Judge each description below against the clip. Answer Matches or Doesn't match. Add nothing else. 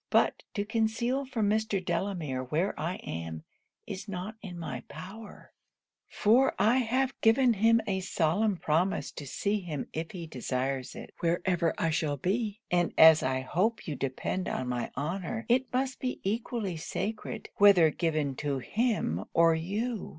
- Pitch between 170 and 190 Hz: Matches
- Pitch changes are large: Matches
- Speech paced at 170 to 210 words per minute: Doesn't match